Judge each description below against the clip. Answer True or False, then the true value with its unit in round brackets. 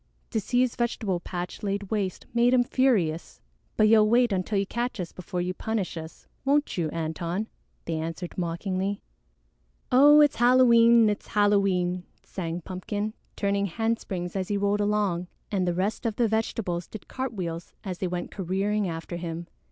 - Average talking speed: True (165 wpm)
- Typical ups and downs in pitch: True (4.1 semitones)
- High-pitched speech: True (200 Hz)